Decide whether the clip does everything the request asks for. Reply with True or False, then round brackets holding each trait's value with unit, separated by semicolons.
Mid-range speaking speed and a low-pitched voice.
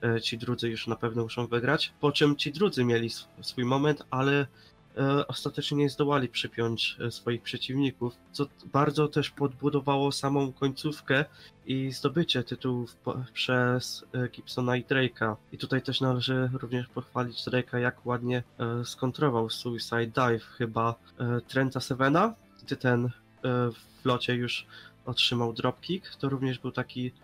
True (130 wpm; 125 Hz)